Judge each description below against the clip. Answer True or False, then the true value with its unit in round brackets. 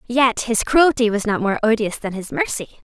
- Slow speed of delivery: False (205 wpm)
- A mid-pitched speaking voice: False (230 Hz)